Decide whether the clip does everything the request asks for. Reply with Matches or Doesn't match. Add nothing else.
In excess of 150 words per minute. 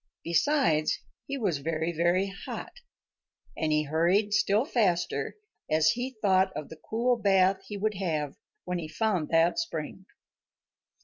Doesn't match